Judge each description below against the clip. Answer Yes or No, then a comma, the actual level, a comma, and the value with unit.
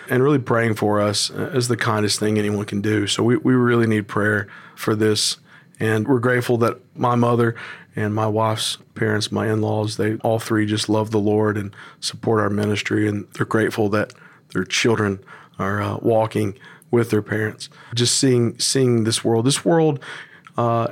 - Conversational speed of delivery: Yes, average, 185 wpm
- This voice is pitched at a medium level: No, low, 110 Hz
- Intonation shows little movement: Yes, narrow, 2.3 semitones